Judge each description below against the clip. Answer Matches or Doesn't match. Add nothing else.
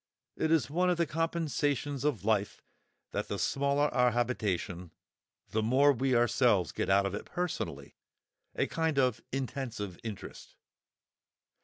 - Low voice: Matches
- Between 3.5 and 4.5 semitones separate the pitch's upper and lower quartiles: Doesn't match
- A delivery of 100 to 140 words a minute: Matches